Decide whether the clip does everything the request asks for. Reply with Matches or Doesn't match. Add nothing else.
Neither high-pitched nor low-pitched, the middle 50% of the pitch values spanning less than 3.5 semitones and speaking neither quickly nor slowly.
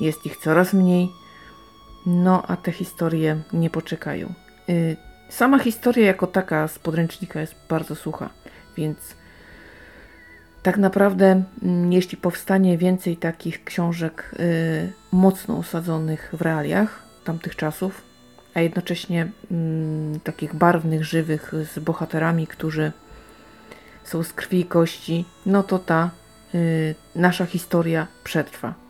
Matches